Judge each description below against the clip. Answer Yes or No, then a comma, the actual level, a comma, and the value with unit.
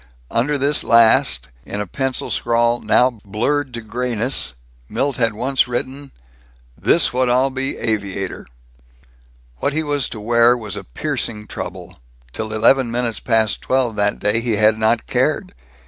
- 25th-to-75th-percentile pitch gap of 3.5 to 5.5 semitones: No, average, 3.1 semitones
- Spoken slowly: No, average, 150 wpm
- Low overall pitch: Yes, low, 120 Hz